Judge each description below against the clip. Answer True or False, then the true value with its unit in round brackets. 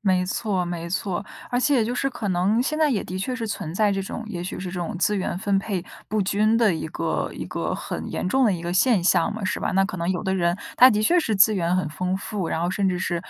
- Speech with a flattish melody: False (3.3 semitones)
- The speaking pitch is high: True (195 Hz)